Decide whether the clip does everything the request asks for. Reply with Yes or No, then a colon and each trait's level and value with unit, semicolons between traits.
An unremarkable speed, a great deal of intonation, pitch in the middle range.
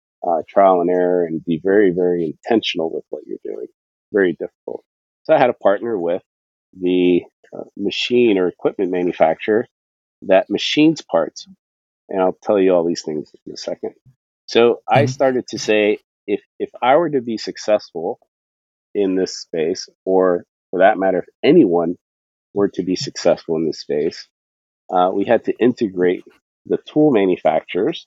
No: average, 160 wpm; wide, 6.1 semitones; very low, 95 Hz